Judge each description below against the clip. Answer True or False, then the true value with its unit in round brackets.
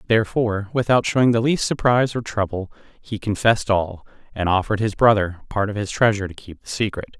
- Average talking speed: True (190 wpm)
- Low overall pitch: True (105 Hz)